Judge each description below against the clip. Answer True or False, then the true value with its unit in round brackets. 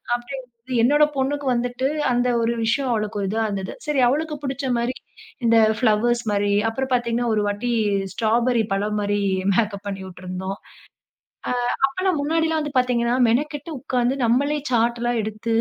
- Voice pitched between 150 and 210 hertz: False (240 Hz)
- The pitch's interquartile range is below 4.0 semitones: True (3.6 semitones)